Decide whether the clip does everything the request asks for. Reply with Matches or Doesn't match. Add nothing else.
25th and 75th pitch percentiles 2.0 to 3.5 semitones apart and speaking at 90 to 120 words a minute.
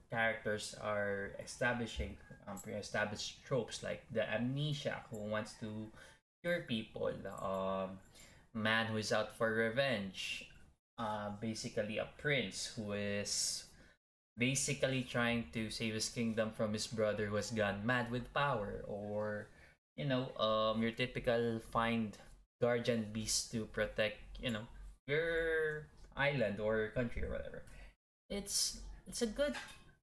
Doesn't match